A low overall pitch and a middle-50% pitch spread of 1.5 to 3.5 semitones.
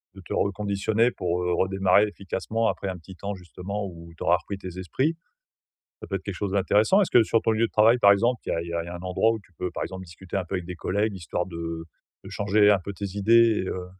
Yes: very low, 95 Hz; average, 2.8 semitones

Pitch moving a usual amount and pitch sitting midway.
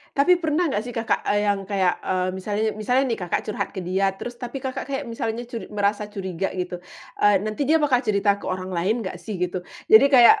No: average, 4.4 semitones; high, 210 Hz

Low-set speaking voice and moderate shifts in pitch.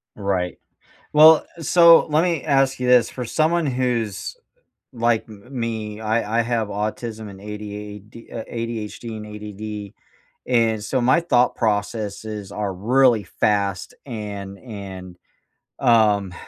Yes: low, 110 Hz; average, 3.0 semitones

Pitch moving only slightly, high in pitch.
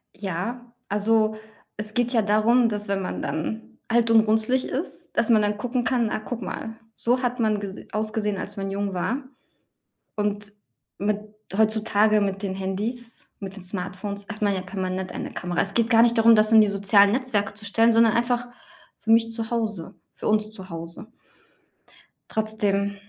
Yes: narrow, 2.3 semitones; high, 215 Hz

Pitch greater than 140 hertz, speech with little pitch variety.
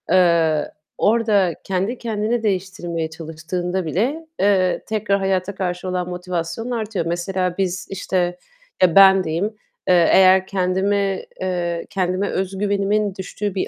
Yes: medium, 185 Hz; narrow, 2.2 semitones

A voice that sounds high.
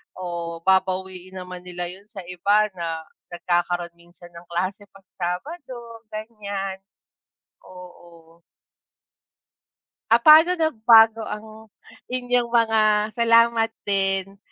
Yes: high, 195 Hz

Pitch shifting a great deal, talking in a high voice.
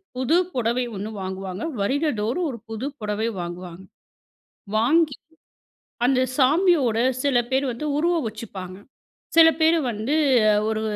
Yes: wide, 5.9 semitones; high, 240 Hz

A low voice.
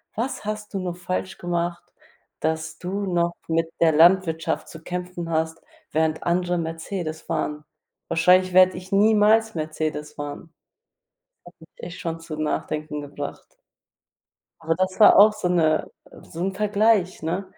No: medium, 175 Hz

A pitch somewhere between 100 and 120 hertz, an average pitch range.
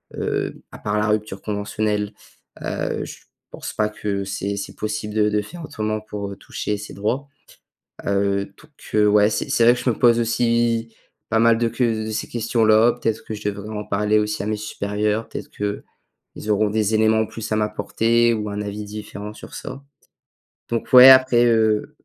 No: low, 105 Hz; narrow, 1.7 semitones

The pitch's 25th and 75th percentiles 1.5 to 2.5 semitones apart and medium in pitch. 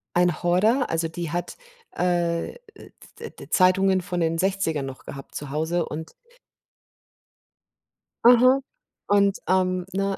No: average, 2.9 semitones; medium, 180 Hz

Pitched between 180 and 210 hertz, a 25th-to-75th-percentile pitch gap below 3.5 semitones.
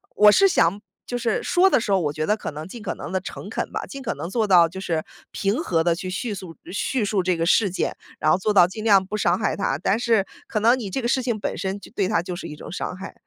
No: high, 195 Hz; average, 4.1 semitones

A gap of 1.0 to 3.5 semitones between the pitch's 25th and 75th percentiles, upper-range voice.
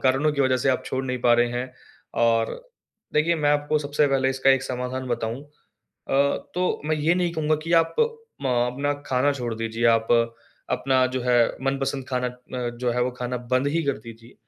No: average, 2.8 semitones; low, 130 Hz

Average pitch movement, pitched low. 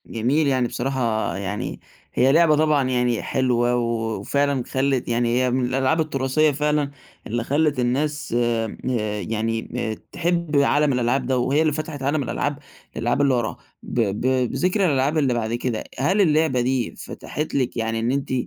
Yes: average, 3.4 semitones; low, 130 Hz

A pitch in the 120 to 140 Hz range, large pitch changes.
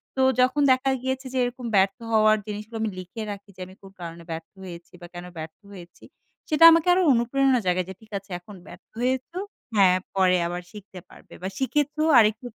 No: high, 210 Hz; wide, 6.0 semitones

